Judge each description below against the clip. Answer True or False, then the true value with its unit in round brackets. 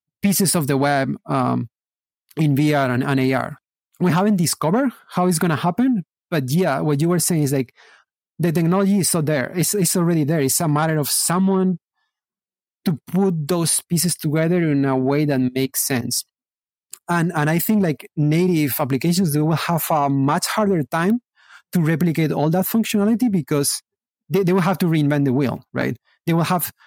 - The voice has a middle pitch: True (165 Hz)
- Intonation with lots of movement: False (4.1 semitones)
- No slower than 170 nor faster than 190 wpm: True (185 wpm)